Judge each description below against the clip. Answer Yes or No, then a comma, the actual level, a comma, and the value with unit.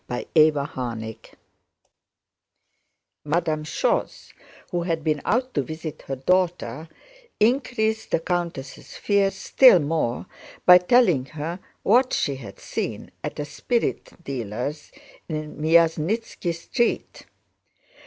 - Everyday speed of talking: No, slow, 105 wpm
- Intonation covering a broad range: No, average, 4.7 semitones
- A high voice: No, medium, 160 Hz